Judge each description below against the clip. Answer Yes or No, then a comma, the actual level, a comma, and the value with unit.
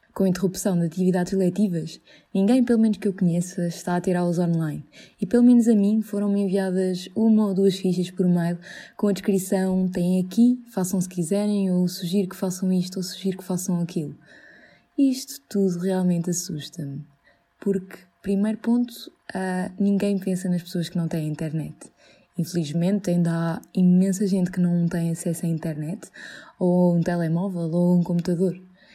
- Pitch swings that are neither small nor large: No, narrow, 2.3 semitones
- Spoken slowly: No, average, 165 wpm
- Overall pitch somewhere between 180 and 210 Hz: Yes, medium, 185 Hz